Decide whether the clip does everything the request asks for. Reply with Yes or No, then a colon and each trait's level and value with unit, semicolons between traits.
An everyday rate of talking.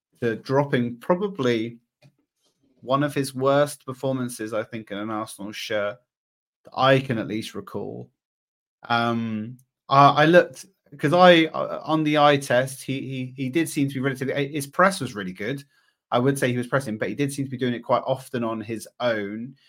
Yes: average, 190 wpm